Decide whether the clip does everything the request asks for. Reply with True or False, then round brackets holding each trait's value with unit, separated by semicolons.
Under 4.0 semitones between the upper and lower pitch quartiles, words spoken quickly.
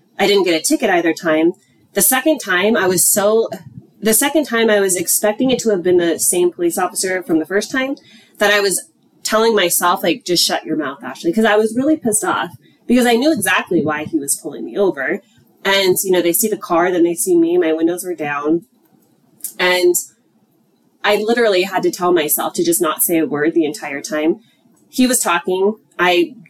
False (4.6 semitones; 210 wpm)